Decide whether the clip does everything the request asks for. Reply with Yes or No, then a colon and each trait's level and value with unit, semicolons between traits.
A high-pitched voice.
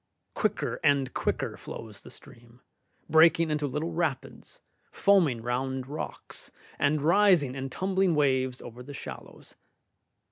No: medium, 140 Hz